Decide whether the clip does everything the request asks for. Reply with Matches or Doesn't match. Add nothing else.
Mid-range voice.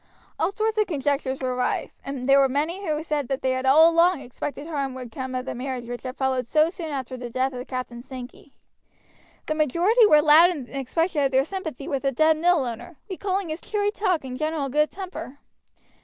Doesn't match